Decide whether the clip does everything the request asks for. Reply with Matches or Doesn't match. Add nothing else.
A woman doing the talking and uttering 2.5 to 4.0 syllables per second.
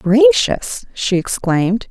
Matches